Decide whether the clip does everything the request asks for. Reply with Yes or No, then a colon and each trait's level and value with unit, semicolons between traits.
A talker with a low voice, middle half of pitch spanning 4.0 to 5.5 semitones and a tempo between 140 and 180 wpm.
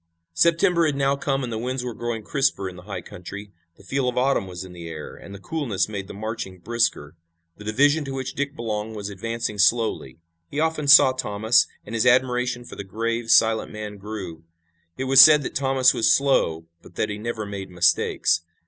No: low, 115 Hz; average, 4.8 semitones; fast, 205 wpm